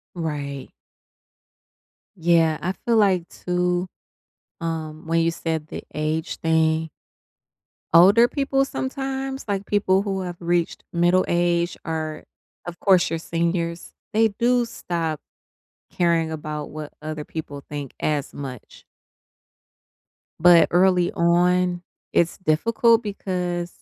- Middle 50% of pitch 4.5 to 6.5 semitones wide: No, average, 2.8 semitones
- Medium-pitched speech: Yes, medium, 170 Hz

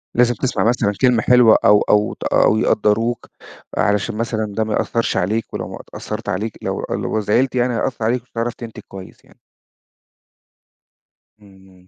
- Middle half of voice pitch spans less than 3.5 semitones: Yes, narrow, 2.5 semitones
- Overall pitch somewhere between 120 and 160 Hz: No, low, 110 Hz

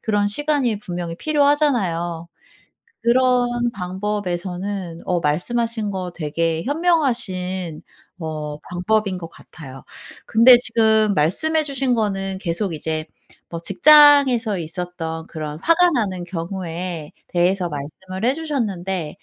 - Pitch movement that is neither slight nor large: No, wide, 6.0 semitones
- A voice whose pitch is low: No, high, 190 Hz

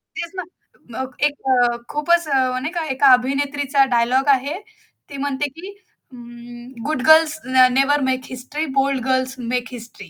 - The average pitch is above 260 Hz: Yes, very high, 270 Hz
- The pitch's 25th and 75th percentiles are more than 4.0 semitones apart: No, narrow, 2.6 semitones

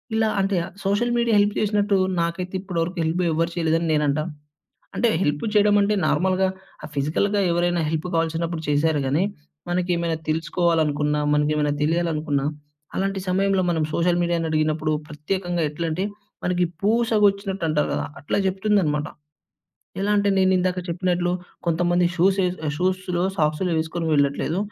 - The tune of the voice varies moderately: Yes, average, 3.2 semitones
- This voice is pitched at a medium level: Yes, medium, 175 Hz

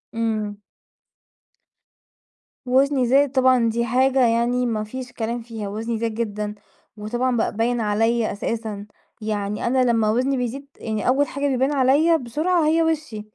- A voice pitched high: Yes, high, 235 Hz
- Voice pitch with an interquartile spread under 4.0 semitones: Yes, average, 3.2 semitones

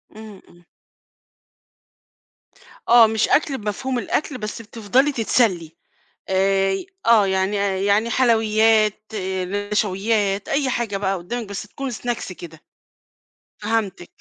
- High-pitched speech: Yes, high, 215 Hz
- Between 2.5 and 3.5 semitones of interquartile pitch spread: Yes, average, 3.2 semitones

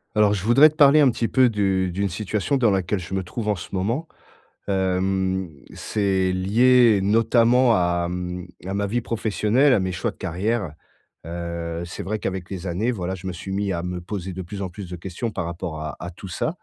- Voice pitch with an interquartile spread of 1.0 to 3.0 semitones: No, average, 3.6 semitones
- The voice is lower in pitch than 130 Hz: Yes, very low, 95 Hz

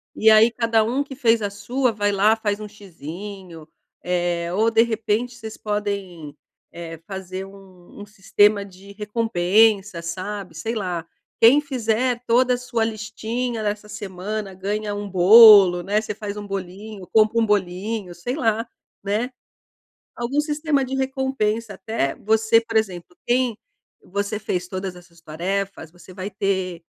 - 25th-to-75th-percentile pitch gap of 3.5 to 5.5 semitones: No, average, 3.1 semitones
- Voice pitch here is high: Yes, high, 210 Hz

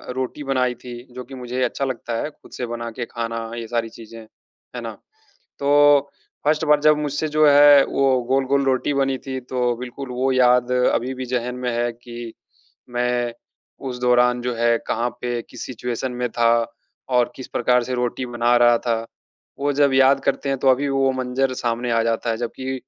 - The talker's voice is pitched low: Yes, low, 125 Hz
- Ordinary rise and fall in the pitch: No, narrow, 2.0 semitones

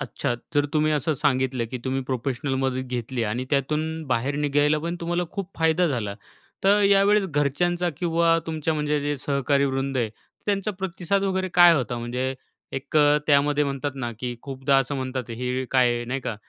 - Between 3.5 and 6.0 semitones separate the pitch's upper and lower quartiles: Yes, average, 3.9 semitones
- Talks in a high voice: No, medium, 140 Hz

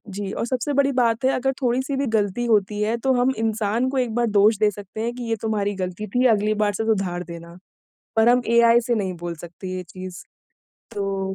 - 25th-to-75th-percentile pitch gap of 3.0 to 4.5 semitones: Yes, average, 3.6 semitones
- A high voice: Yes, high, 215 Hz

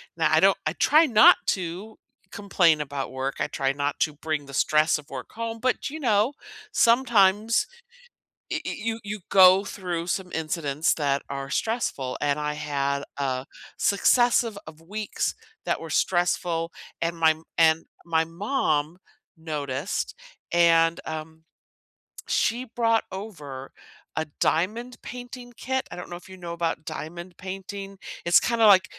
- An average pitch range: No, wide, 5.7 semitones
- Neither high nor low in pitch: Yes, medium, 175 Hz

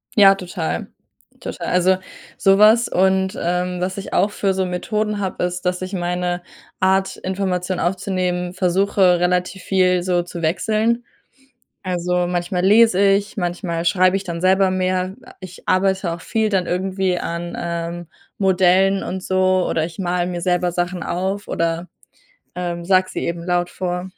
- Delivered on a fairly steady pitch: Yes, narrow, 1.4 semitones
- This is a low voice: No, medium, 185 Hz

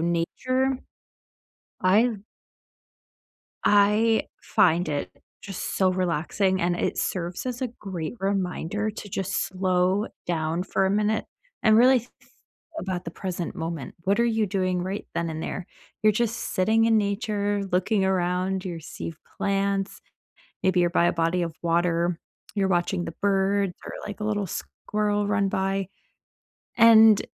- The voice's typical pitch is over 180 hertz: Yes, high, 190 Hz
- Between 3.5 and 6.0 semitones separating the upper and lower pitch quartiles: No, average, 2.9 semitones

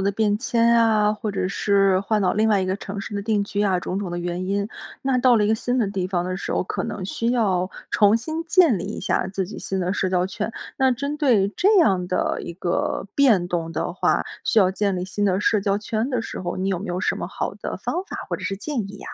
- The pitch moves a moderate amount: Yes, average, 3.3 semitones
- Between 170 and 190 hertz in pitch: No, high, 200 Hz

